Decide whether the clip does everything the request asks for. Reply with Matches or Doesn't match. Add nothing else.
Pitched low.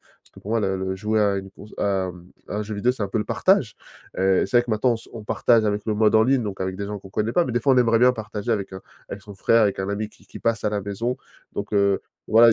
Matches